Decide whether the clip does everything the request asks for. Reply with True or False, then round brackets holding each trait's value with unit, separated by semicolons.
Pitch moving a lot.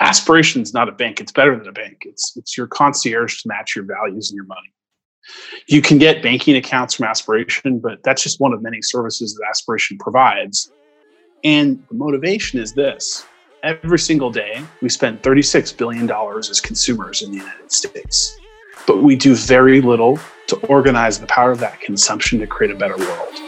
True (6.2 semitones)